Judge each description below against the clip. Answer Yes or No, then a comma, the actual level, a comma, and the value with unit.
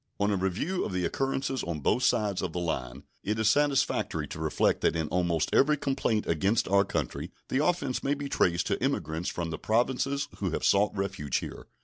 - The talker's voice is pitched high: No, low, 100 Hz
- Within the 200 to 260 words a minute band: Yes, fast, 205 wpm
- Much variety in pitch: Yes, wide, 7.9 semitones